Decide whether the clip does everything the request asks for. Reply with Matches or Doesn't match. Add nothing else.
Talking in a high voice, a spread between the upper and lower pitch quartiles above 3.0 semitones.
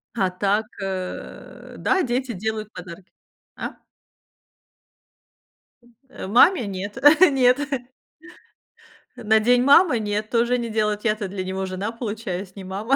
Matches